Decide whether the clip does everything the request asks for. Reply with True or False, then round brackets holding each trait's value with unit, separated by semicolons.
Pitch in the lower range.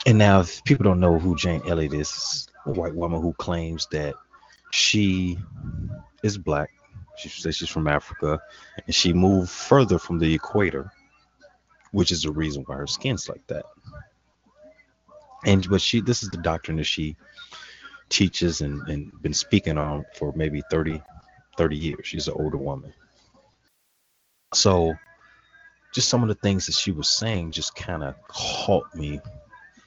True (85 Hz)